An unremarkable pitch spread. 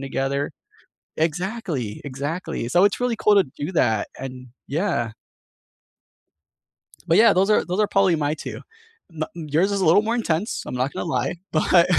No: wide, 5.9 semitones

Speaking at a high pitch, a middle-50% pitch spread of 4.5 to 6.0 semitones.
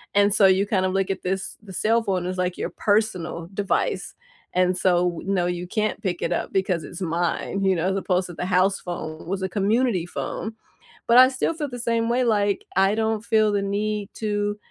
No: high, 195 Hz; average, 2.8 semitones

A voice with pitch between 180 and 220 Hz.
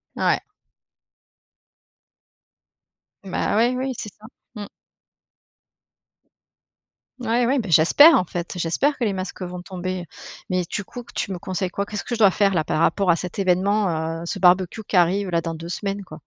Yes: high, 190 Hz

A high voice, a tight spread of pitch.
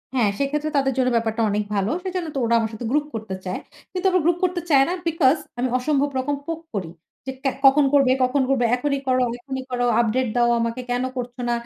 No: very high, 260 Hz; average, 3.4 semitones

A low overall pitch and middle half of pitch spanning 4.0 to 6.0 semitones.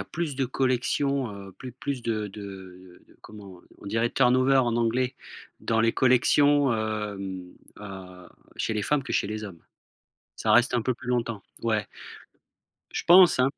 Yes: low, 115 Hz; average, 4.3 semitones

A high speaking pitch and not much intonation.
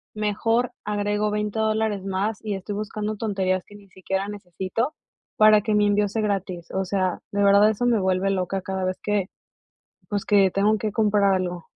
Yes: high, 205 Hz; narrow, 1.8 semitones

